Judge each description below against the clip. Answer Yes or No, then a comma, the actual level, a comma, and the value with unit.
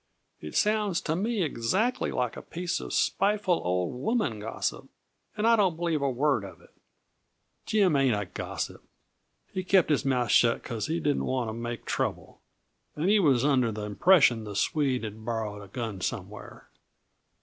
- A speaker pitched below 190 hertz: Yes, low, 135 Hz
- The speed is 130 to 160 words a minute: No, average, 170 wpm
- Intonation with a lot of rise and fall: Yes, wide, 8.3 semitones